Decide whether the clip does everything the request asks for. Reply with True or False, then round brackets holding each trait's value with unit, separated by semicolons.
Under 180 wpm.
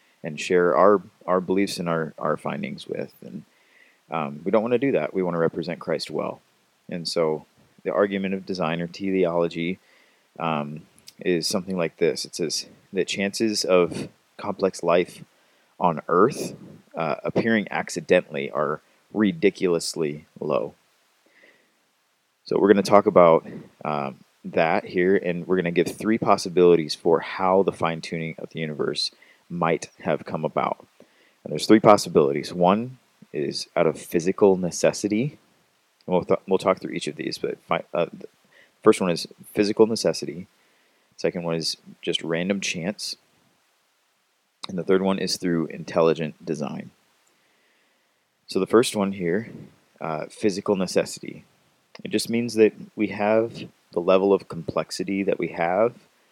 True (150 wpm)